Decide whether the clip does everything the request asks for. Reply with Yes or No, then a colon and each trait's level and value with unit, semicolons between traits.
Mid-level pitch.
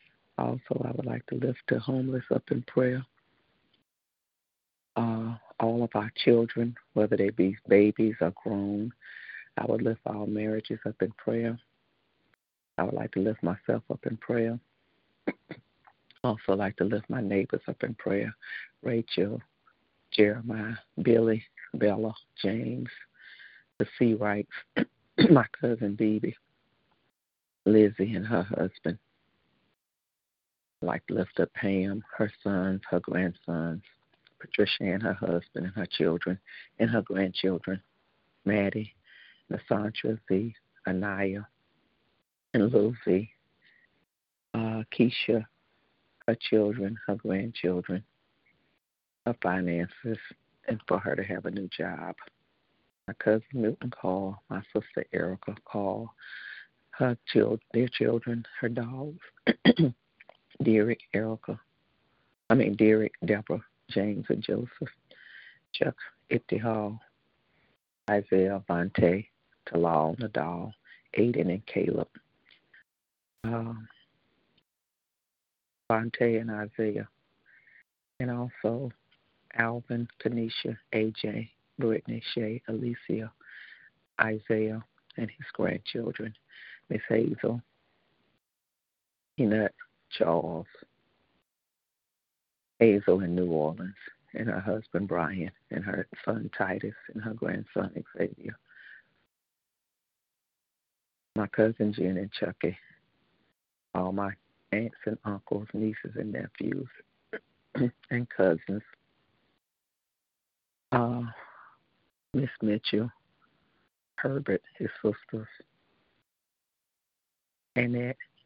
No: low, 110 Hz